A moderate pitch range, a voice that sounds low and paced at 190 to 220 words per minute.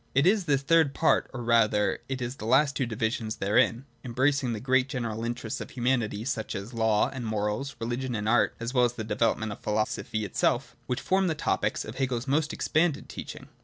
Yes: average, 3.6 semitones; low, 120 Hz; fast, 205 wpm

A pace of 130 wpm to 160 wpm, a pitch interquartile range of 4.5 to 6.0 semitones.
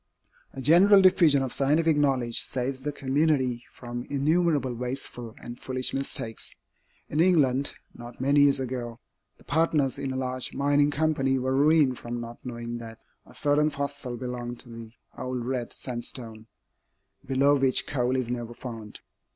No: average, 150 wpm; average, 2.9 semitones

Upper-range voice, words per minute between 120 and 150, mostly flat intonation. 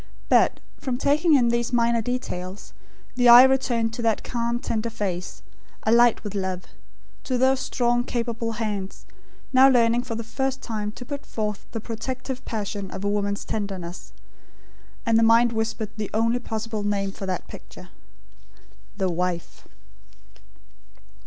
No: high, 230 Hz; average, 145 wpm; average, 3.0 semitones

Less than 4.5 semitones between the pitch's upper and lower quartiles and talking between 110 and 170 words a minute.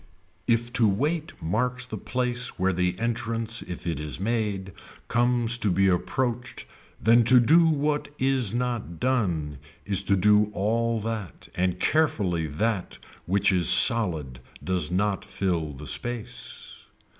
No: average, 4.9 semitones; average, 140 wpm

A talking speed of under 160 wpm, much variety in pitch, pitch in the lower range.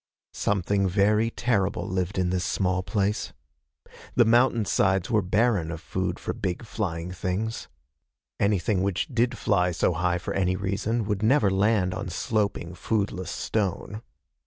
No: average, 140 wpm; average, 2.9 semitones; low, 100 Hz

